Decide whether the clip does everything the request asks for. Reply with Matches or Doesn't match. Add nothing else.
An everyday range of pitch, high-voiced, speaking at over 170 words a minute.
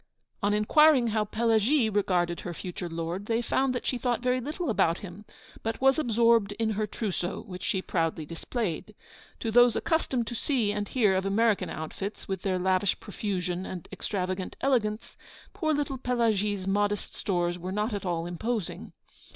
Doesn't match